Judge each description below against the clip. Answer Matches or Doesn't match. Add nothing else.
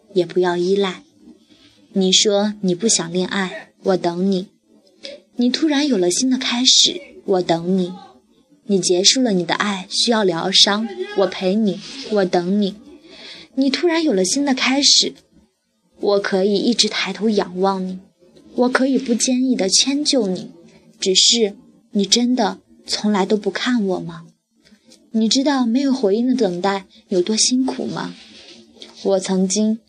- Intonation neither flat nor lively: Matches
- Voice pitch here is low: Doesn't match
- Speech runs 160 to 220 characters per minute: Matches